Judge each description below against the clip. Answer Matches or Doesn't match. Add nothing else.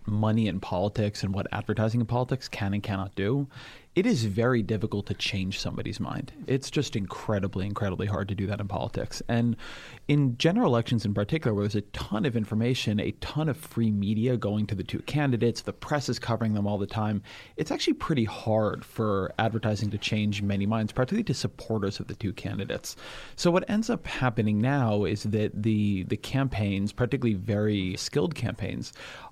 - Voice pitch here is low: Matches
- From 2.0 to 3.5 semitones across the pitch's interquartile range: Matches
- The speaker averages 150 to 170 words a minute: Doesn't match